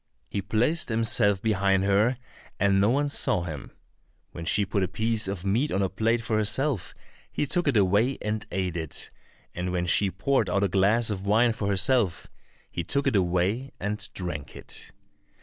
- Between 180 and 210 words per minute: Yes, average, 185 wpm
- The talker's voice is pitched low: Yes, low, 100 Hz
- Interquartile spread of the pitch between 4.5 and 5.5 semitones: No, average, 3.4 semitones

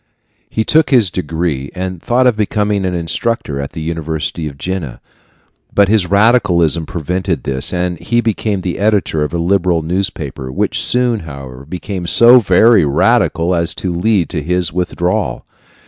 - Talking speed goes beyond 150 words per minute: Yes, average, 160 wpm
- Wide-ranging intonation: No, average, 4.2 semitones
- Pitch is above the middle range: No, very low, 90 Hz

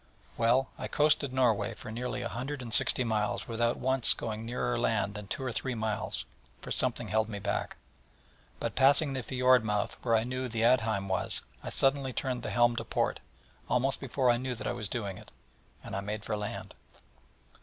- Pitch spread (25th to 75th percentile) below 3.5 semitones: Yes, average, 2.9 semitones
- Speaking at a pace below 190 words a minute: No, average, 195 wpm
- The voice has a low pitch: Yes, low, 120 Hz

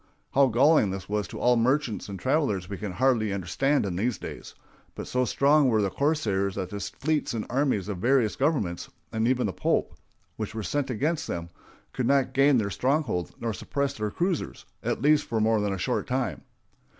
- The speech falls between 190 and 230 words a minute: Yes, average, 200 wpm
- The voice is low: Yes, low, 115 Hz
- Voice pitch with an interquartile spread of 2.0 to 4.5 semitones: No, wide, 5.5 semitones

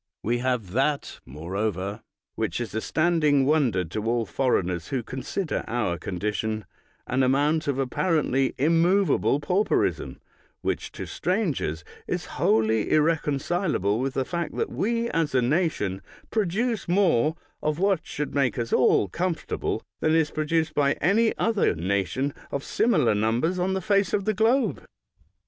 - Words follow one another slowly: No, average, 150 wpm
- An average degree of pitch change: No, wide, 7.6 semitones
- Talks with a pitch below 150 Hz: Yes, medium, 140 Hz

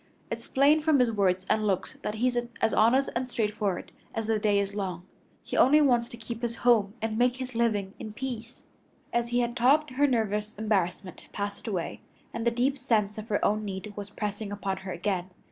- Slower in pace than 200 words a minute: No, fast, 205 wpm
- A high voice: Yes, high, 220 Hz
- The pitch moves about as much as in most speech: Yes, average, 3.1 semitones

